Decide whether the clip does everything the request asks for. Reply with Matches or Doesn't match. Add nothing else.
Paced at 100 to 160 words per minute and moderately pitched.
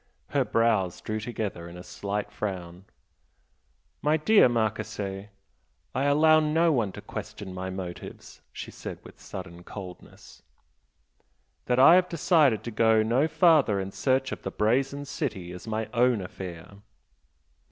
Doesn't match